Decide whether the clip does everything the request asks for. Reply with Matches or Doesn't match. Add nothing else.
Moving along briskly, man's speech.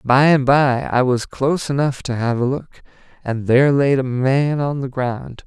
Matches